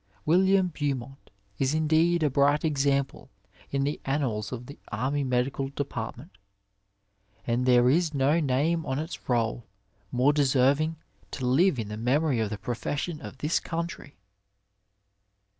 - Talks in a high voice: No, medium, 140 Hz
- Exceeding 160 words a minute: No, average, 140 wpm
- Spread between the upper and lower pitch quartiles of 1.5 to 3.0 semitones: No, average, 3.7 semitones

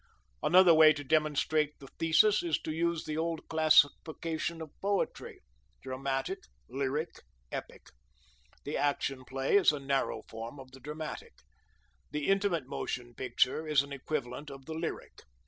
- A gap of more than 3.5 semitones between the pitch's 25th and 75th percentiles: No, average, 2.9 semitones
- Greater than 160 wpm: No, average, 145 wpm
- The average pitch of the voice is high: No, medium, 150 Hz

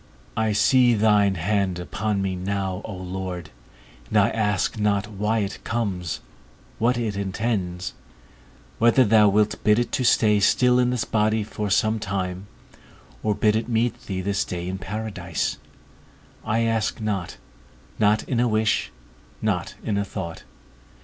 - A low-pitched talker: Yes, low, 105 Hz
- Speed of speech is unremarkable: Yes, average, 150 wpm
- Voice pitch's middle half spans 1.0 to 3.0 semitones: Yes, narrow, 2.6 semitones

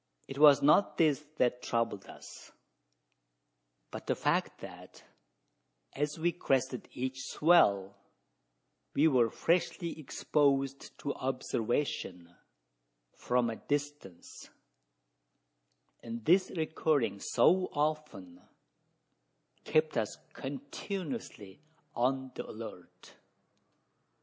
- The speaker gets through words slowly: Yes, slow, 90 wpm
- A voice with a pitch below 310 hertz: Yes, low, 135 Hz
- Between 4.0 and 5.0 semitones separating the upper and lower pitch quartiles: Yes, average, 4.7 semitones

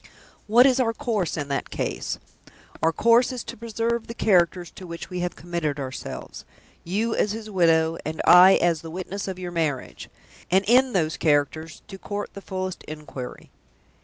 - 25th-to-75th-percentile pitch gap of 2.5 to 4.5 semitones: No, average, 5.1 semitones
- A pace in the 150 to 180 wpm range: Yes, average, 175 wpm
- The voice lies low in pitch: No, medium, 180 Hz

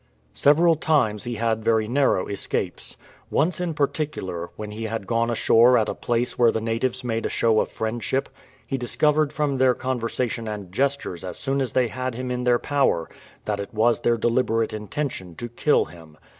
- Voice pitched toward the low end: Yes, low, 120 Hz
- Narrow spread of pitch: No, average, 3.4 semitones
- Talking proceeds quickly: No, average, 190 wpm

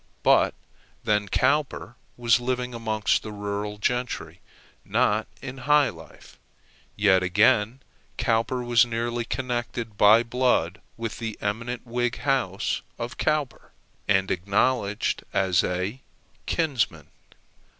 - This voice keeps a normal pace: No, slow, 110 wpm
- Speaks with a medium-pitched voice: No, low, 115 Hz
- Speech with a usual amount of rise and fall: Yes, average, 3.3 semitones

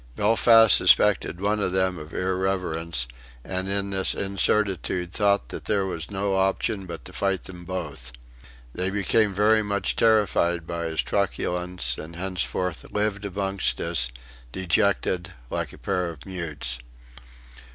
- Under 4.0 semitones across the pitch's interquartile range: Yes, average, 2.8 semitones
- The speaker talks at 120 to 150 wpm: Yes, average, 140 wpm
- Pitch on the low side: Yes, very low, 95 Hz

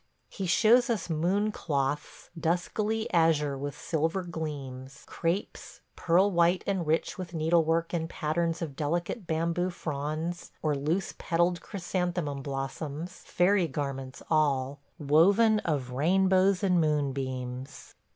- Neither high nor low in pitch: Yes, medium, 165 Hz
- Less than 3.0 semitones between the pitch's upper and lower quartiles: No, average, 3.6 semitones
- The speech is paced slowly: Yes, slow, 120 wpm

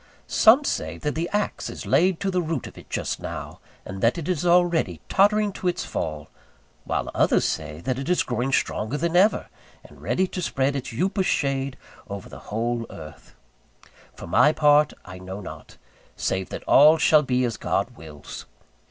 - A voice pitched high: No, medium, 140 Hz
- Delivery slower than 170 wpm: No, average, 185 wpm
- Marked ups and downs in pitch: Yes, wide, 8.4 semitones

